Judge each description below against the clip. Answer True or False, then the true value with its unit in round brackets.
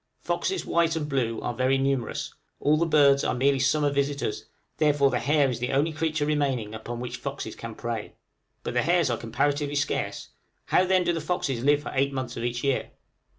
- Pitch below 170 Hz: True (140 Hz)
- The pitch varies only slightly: False (3.1 semitones)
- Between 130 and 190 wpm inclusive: False (200 wpm)